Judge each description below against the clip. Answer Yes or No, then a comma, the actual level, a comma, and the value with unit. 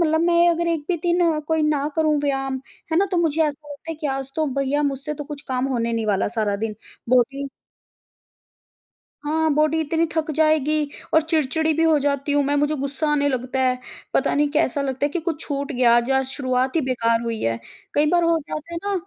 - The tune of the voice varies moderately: Yes, average, 3.2 semitones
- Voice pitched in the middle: No, very high, 290 Hz